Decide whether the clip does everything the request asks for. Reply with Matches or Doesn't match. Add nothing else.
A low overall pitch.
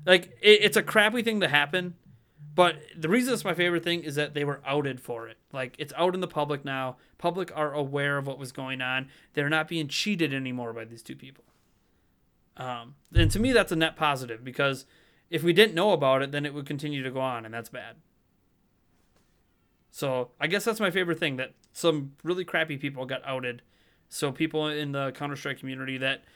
Doesn't match